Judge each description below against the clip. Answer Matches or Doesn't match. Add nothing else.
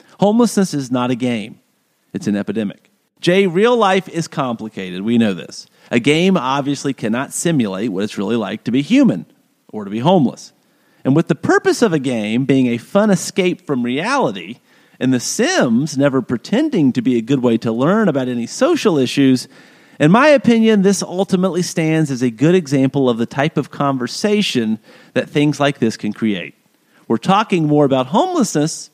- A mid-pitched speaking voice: Matches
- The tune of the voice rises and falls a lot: Matches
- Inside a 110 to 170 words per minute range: Doesn't match